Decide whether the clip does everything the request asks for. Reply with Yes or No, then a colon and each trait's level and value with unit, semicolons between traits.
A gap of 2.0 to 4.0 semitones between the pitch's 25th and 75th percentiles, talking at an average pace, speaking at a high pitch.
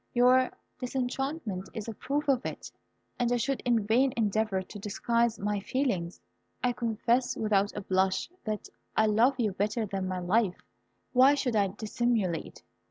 Yes: average, 3.5 semitones; average, 155 wpm; high, 225 Hz